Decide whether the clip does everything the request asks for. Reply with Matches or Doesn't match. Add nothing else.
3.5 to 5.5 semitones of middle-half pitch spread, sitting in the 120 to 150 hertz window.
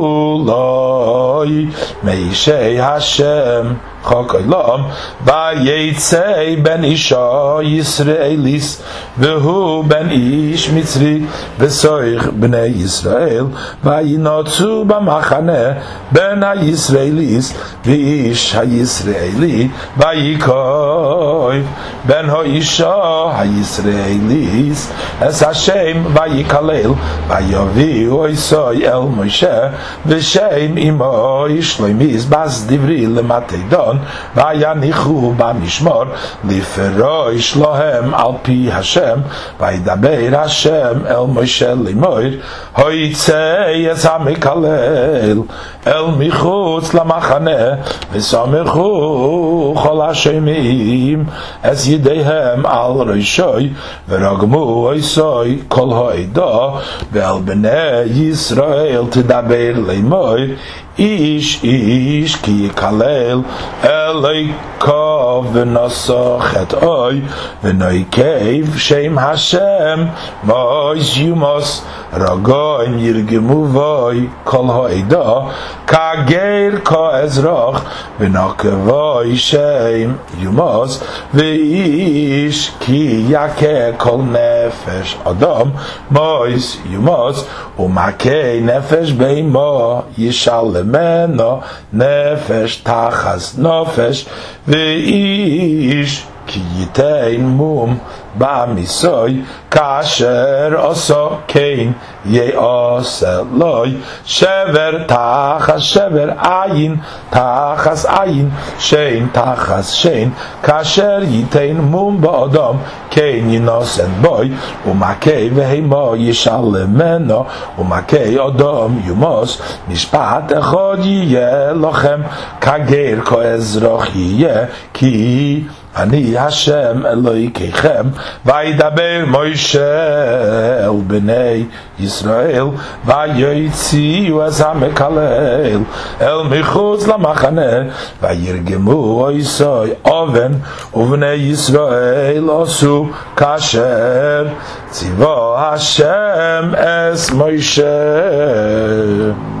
Matches